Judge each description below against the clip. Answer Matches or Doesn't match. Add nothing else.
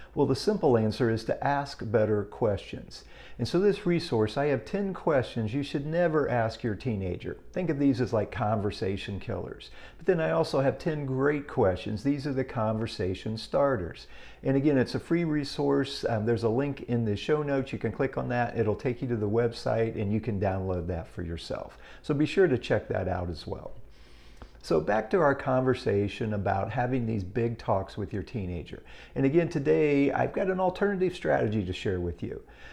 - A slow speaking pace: Doesn't match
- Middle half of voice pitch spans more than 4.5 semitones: Matches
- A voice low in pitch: Matches